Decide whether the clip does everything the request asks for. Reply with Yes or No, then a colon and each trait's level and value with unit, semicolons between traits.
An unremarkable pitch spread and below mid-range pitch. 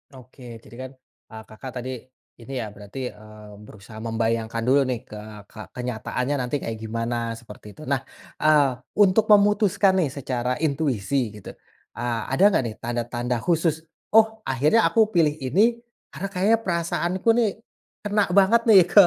No: wide, 8.1 semitones; low, 130 Hz